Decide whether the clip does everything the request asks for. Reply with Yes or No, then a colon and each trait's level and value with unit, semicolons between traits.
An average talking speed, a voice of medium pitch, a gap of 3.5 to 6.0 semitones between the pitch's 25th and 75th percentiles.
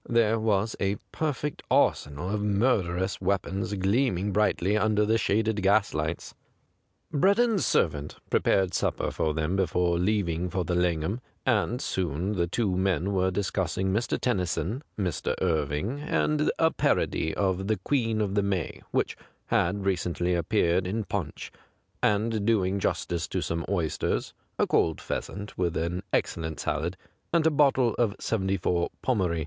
No: average, 150 wpm; very low, 95 Hz; average, 3.8 semitones